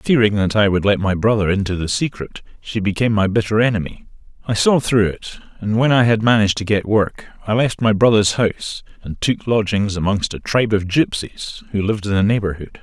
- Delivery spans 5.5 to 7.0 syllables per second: Yes, 5.6 syllables/s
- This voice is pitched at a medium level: No, low, 105 Hz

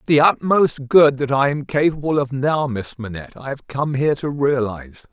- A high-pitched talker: No, low, 135 Hz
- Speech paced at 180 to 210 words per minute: Yes, average, 200 wpm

